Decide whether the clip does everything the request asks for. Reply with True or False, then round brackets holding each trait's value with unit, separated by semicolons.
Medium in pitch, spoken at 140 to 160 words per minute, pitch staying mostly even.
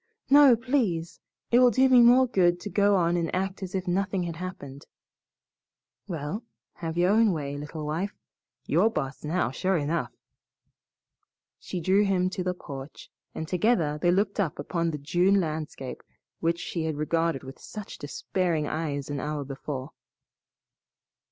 False (175 Hz; 155 wpm; 4.5 semitones)